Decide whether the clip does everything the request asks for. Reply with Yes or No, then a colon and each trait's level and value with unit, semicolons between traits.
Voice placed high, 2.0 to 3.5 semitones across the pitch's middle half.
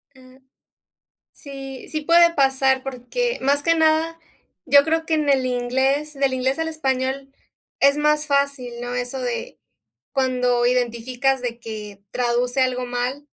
Yes: very high, 265 Hz; narrow, 2.6 semitones